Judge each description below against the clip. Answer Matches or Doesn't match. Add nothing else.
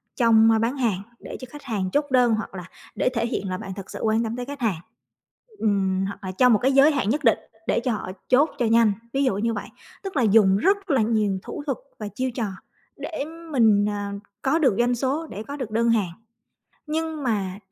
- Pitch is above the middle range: Matches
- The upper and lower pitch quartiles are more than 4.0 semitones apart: Matches